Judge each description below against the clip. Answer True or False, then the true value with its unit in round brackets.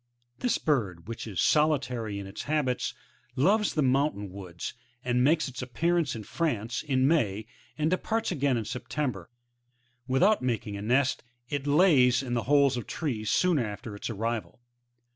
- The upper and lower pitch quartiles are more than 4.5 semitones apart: True (5.3 semitones)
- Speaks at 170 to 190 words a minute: False (155 wpm)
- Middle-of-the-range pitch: False (130 Hz)